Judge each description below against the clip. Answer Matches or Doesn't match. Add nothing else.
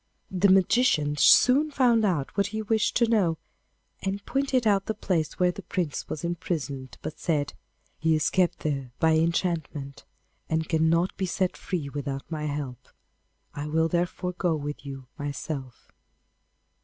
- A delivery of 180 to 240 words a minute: Doesn't match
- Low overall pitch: Doesn't match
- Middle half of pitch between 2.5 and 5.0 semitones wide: Matches